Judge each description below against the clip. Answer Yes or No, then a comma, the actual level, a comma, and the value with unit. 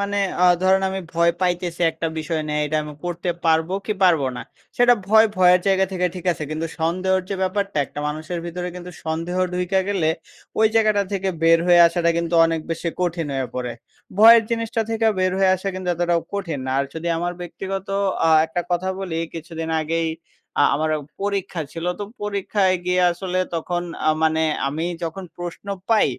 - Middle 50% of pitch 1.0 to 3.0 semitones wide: Yes, average, 2.7 semitones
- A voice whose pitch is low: No, medium, 175 Hz